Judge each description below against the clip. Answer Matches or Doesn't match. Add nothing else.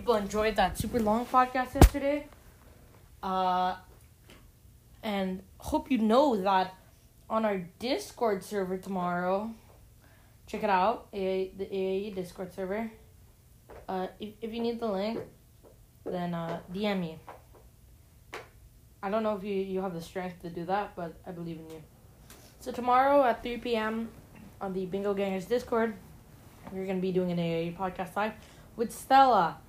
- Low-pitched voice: Doesn't match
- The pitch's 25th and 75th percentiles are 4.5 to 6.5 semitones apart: Doesn't match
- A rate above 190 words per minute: Doesn't match